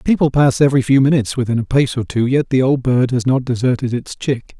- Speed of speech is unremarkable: No, fast, 250 wpm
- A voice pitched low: Yes, low, 130 Hz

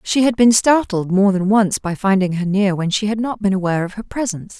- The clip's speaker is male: No, female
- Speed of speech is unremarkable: No, fast, 260 wpm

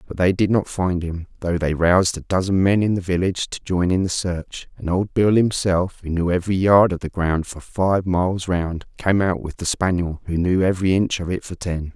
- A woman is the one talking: No, male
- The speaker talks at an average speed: No, fast, 240 wpm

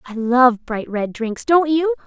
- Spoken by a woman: Yes, female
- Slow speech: No, fast, 205 wpm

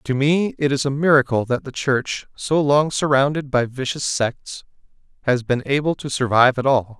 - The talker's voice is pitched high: No, low, 135 Hz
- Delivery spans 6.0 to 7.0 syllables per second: No, 4.8 syllables/s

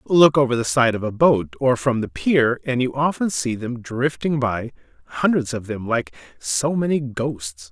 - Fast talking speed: No, average, 195 wpm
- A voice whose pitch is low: Yes, low, 125 Hz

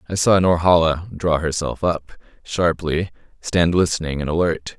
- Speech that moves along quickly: No, average, 140 wpm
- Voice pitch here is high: No, very low, 85 Hz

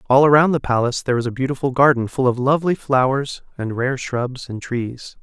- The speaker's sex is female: No, male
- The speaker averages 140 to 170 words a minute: No, fast, 205 wpm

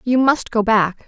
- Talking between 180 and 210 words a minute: No, fast, 225 wpm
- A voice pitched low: No, high, 230 Hz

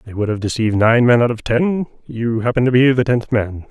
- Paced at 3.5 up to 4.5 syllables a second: No, 5.7 syllables/s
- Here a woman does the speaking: No, male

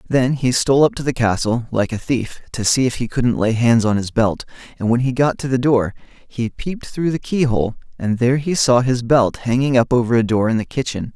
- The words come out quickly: Yes, fast, 250 wpm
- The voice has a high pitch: No, low, 125 Hz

